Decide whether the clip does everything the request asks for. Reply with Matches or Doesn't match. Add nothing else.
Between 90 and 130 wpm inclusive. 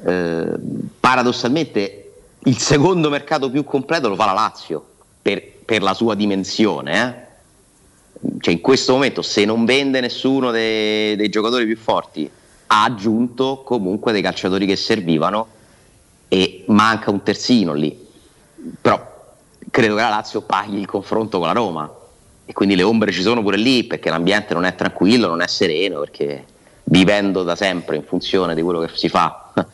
Doesn't match